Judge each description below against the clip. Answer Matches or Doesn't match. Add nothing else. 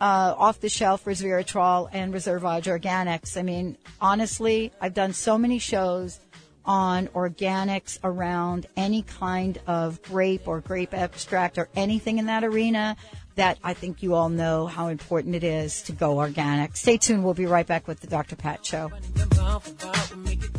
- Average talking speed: Matches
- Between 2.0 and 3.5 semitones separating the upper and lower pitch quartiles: Matches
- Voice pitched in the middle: Matches